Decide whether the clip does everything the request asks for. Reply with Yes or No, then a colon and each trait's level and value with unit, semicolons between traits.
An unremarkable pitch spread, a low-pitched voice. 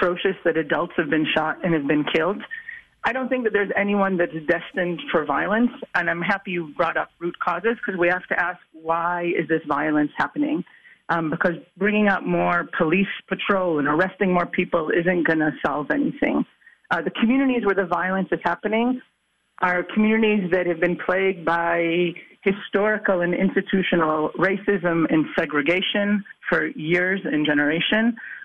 No: average, 3.1 semitones; medium, 180 Hz